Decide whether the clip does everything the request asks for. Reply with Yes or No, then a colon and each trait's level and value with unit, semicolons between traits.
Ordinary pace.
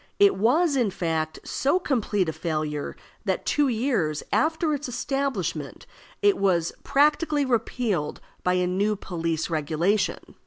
No: slow, 130 wpm